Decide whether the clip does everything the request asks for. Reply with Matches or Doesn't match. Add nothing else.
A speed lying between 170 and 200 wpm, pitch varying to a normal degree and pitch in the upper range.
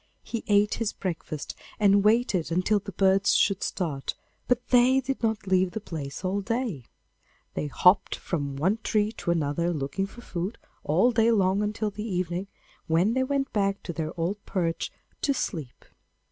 Matches